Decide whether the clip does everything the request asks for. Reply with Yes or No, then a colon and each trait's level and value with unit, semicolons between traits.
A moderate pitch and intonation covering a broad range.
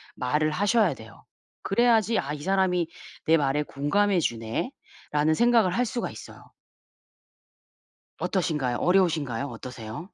Yes: medium, 160 Hz; wide, 6.2 semitones